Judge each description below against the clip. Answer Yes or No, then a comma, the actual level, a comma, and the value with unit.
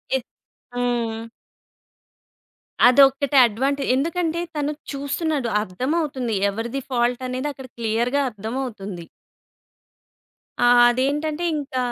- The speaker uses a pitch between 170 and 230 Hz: No, very high, 260 Hz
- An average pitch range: Yes, average, 3.1 semitones